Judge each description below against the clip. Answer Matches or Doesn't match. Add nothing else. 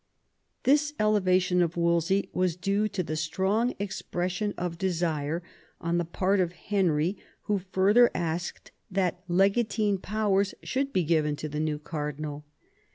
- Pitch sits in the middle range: Matches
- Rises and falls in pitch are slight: Doesn't match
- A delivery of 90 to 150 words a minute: Matches